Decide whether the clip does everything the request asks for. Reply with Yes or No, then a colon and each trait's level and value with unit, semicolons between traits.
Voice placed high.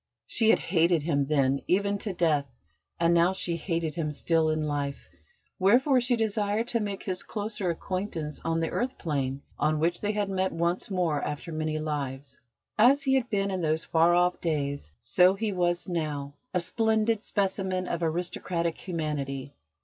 No: medium, 170 Hz